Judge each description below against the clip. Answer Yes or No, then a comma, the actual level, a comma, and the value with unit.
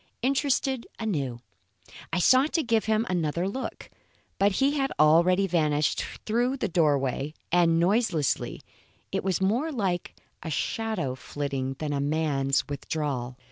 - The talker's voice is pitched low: No, medium, 175 Hz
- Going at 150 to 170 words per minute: No, average, 140 wpm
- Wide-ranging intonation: Yes, wide, 7.3 semitones